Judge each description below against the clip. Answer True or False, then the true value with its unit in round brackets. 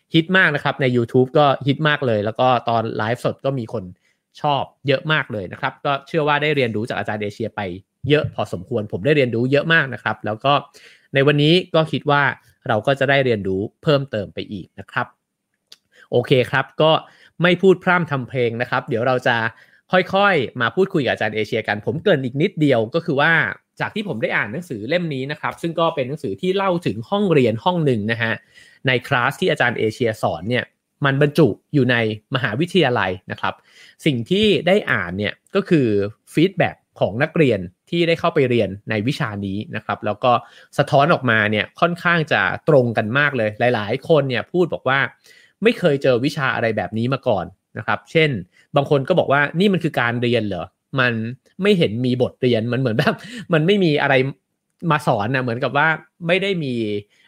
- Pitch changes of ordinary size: False (5.7 semitones)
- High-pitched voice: False (135 Hz)